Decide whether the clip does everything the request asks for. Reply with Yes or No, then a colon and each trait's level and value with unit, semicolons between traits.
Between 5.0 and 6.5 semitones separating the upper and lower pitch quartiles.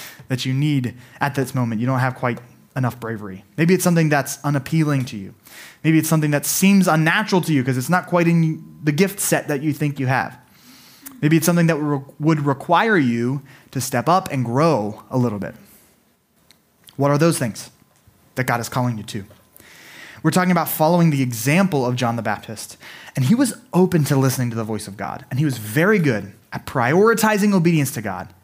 Yes: average, 5.3 semitones